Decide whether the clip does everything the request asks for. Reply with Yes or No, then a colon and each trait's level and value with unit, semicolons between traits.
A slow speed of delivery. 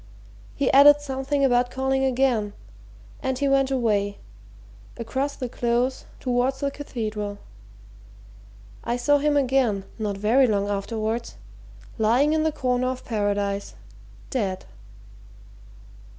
Yes: slow, 115 wpm